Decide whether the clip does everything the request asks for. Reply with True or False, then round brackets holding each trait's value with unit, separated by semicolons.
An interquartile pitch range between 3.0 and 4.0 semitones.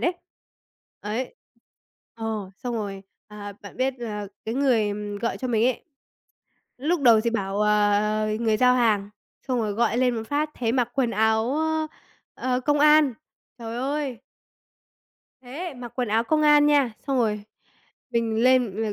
True (3.3 semitones)